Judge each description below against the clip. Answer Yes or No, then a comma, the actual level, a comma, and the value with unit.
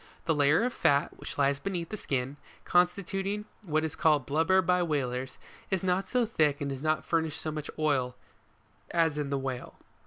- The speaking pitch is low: No, medium, 155 Hz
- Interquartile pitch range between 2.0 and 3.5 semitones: No, average, 4.2 semitones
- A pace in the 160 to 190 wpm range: Yes, average, 185 wpm